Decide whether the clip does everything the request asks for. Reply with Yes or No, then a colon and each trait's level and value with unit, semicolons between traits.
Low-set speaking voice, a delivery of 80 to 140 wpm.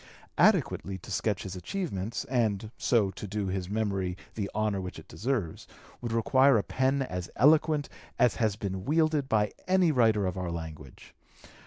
No: low, 105 Hz; average, 165 wpm